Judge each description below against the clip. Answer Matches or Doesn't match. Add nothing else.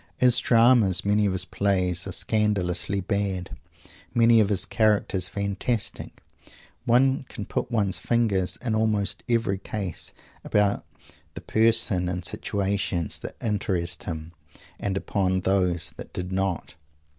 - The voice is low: Matches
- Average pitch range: Matches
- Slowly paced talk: Matches